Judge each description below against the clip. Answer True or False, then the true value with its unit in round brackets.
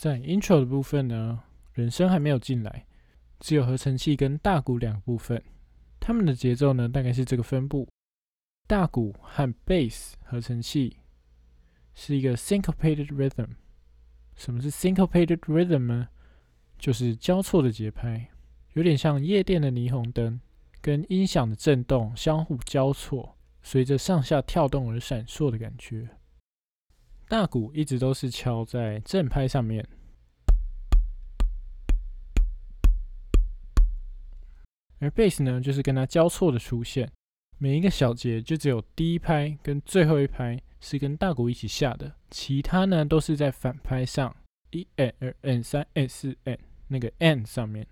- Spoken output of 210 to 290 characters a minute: True (250 characters per minute)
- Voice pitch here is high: False (130 Hz)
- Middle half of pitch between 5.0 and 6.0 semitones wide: True (5.4 semitones)